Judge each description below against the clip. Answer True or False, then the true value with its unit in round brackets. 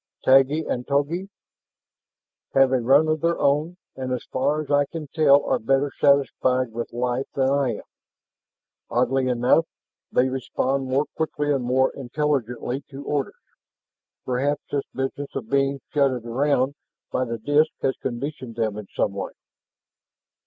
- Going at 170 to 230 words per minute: False (150 wpm)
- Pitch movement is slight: True (2.2 semitones)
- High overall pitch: False (135 Hz)